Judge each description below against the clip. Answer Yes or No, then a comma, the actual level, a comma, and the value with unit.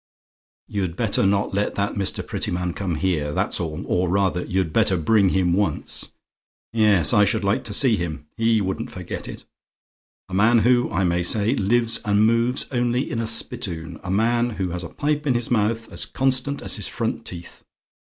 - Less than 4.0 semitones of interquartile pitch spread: No, average, 4.3 semitones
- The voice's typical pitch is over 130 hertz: No, low, 100 Hz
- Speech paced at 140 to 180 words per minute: No, average, 190 wpm